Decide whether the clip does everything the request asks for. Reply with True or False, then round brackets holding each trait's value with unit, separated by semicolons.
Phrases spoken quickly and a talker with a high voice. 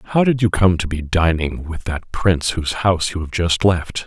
False (235 wpm; 90 Hz)